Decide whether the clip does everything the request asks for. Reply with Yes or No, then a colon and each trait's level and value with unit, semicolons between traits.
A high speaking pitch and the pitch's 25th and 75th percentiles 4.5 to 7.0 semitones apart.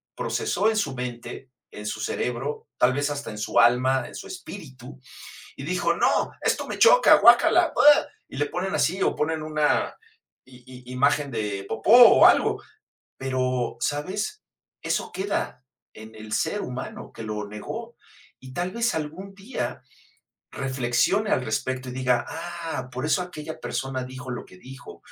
No: low, 135 Hz; wide, 5.5 semitones